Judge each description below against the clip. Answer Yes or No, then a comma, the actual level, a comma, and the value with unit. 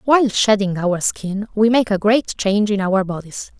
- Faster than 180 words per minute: Yes, average, 200 wpm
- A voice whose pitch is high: Yes, high, 205 Hz